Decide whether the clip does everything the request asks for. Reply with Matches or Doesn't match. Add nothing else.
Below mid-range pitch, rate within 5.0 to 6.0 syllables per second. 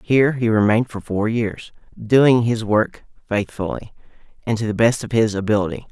Matches